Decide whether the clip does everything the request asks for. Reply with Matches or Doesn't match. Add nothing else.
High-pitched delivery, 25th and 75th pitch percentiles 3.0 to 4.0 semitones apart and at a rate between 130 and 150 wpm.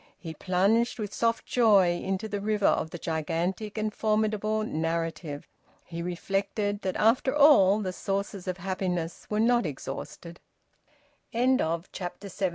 Matches